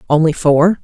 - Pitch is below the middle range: No, medium, 160 Hz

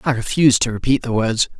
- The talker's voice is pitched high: No, low, 120 Hz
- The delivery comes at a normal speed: No, fast, 225 wpm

